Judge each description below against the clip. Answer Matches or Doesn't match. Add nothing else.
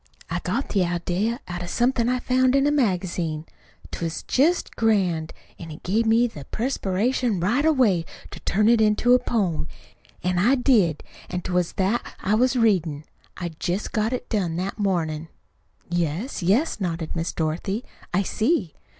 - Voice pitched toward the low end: Doesn't match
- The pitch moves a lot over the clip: Matches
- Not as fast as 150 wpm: Doesn't match